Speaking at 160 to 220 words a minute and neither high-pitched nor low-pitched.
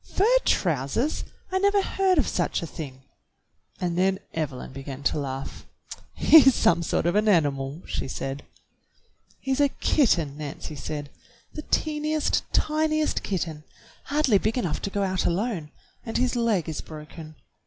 No: average, 150 wpm; medium, 180 Hz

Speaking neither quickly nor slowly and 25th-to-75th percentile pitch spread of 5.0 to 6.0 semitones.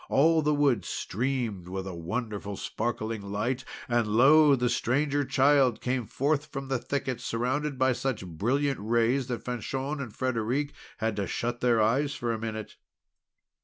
No: average, 160 wpm; average, 3.7 semitones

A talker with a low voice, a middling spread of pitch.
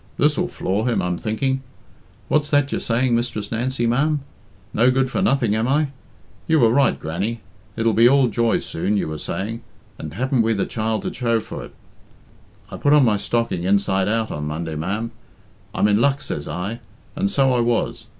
Yes: low, 115 Hz; average, 4.4 semitones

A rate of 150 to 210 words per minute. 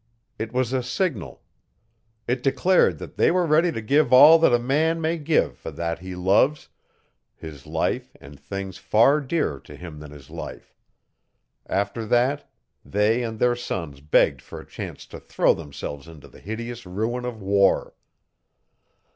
Yes: average, 165 wpm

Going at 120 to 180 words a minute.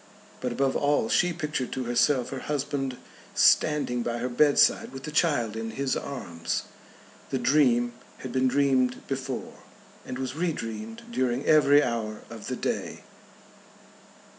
Yes: average, 145 wpm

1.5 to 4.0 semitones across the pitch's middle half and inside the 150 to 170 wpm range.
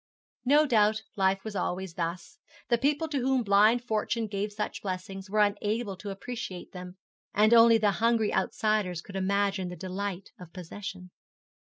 Yes: average, 2.9 semitones; average, 160 wpm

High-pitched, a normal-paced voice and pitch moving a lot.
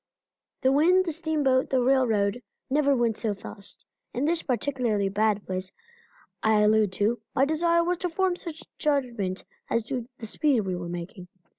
Yes: high, 245 Hz; average, 165 wpm; wide, 6.4 semitones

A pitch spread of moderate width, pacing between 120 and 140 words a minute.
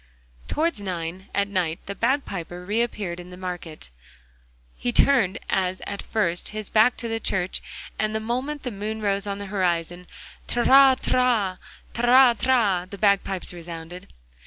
No: average, 4.6 semitones; average, 150 wpm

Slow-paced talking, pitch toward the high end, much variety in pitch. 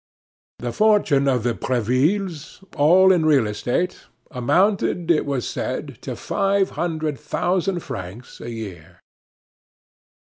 No: slow, 115 wpm; medium, 150 Hz; wide, 6.9 semitones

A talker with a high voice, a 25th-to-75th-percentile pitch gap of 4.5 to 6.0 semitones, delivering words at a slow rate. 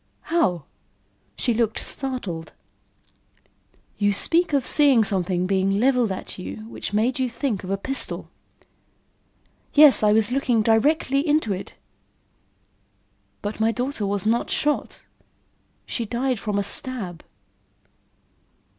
Yes: high, 225 Hz; average, 4.9 semitones; slow, 120 wpm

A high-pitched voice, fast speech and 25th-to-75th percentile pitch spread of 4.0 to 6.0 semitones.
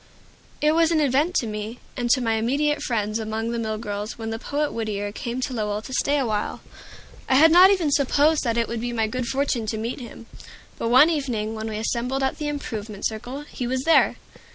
Yes: high, 235 Hz; fast, 215 wpm; average, 4.3 semitones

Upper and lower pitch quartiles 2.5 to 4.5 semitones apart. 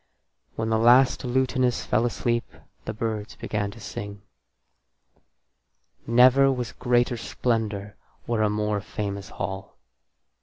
Yes: average, 2.9 semitones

